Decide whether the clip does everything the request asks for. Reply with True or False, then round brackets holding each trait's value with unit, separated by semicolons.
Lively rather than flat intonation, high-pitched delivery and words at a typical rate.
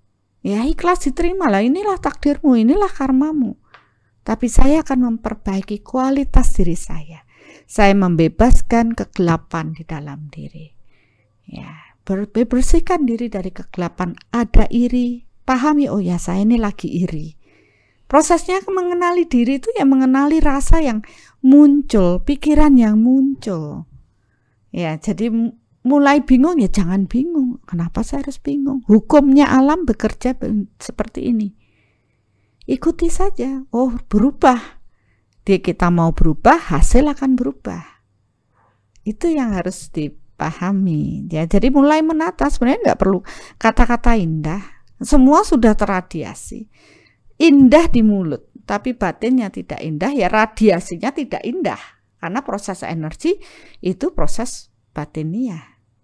True (7.5 semitones; 230 Hz; 115 wpm)